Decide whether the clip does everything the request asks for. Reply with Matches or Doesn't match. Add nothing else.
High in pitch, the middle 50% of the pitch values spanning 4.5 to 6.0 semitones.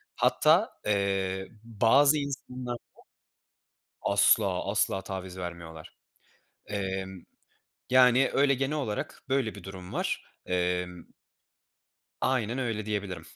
Doesn't match